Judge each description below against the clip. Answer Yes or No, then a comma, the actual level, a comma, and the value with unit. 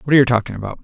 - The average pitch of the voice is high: No, low, 120 Hz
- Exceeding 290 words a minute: Yes, fast, 360 wpm